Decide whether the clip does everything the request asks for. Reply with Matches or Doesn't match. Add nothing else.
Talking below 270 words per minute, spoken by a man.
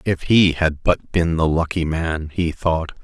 Matches